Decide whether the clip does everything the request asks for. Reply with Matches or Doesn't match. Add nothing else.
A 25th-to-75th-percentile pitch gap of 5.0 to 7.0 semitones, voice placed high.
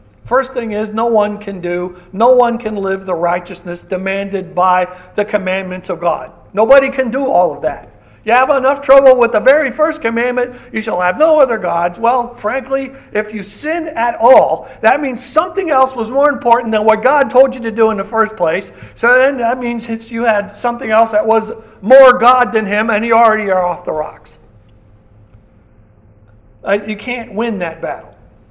Matches